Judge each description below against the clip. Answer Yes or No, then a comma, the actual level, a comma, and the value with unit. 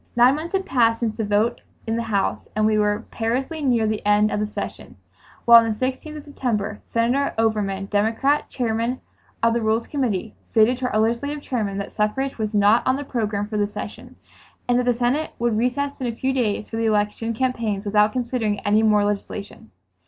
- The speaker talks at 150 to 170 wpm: No, fast, 205 wpm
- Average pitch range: Yes, average, 3.0 semitones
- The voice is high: Yes, high, 225 Hz